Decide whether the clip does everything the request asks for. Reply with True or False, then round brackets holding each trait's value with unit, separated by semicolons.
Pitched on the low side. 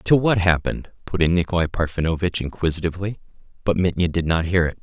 True (85 Hz)